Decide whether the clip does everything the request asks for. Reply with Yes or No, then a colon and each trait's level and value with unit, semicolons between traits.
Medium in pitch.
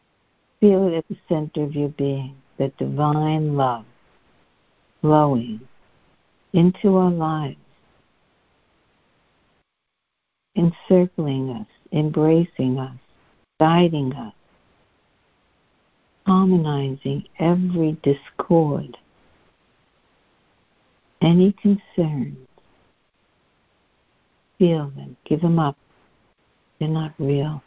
Yes: medium, 155 Hz